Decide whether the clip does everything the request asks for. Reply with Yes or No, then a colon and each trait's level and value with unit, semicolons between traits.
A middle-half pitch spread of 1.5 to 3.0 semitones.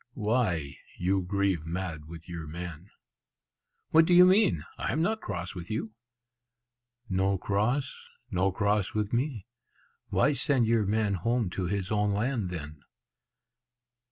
No: average, 4.8 semitones